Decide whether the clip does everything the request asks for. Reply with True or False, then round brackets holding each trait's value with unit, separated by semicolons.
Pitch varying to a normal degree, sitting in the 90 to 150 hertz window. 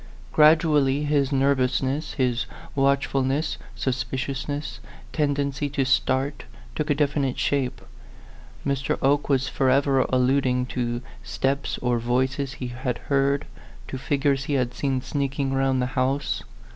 False (1.6 semitones; 135 Hz)